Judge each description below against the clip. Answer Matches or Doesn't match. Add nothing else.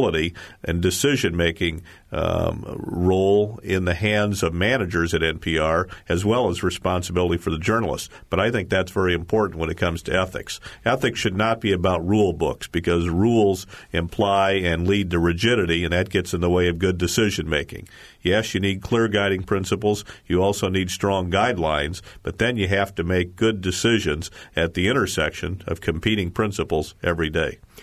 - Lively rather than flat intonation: Doesn't match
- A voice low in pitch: Matches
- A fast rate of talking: Doesn't match